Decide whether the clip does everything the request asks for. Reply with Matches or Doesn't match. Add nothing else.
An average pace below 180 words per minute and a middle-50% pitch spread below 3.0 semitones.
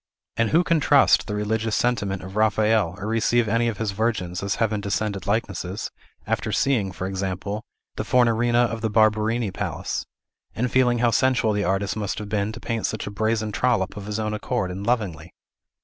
Doesn't match